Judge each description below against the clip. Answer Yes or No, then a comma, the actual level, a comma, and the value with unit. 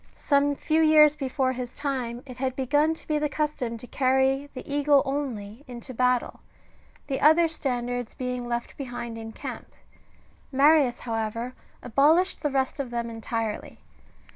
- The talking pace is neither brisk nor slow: Yes, average, 155 wpm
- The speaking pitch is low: No, very high, 260 Hz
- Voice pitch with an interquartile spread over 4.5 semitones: No, average, 3.1 semitones